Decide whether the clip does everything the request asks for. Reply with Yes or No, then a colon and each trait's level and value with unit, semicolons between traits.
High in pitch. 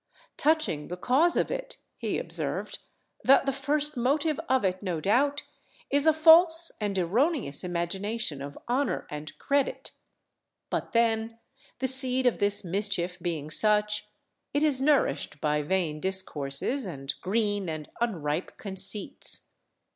Yes: high, 210 Hz